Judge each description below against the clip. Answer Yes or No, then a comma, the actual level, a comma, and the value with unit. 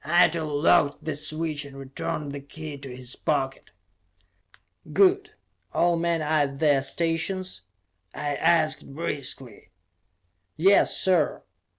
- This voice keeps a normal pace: No, slow, 115 wpm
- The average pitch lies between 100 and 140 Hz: No, medium, 155 Hz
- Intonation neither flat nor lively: Yes, average, 3.2 semitones